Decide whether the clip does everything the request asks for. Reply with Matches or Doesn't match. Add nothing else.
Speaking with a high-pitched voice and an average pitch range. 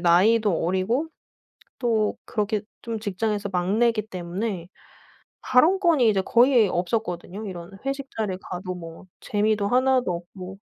Matches